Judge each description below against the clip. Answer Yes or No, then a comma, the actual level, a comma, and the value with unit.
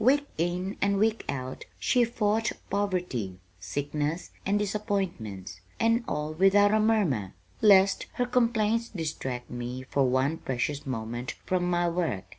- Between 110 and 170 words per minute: Yes, slow, 135 wpm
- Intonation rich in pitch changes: Yes, wide, 8.1 semitones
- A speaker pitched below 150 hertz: No, medium, 175 Hz